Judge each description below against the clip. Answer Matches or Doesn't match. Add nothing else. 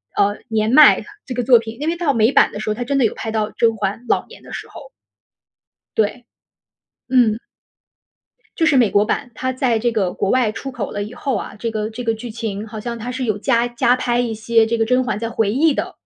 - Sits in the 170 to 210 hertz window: Doesn't match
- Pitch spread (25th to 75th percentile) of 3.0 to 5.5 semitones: Doesn't match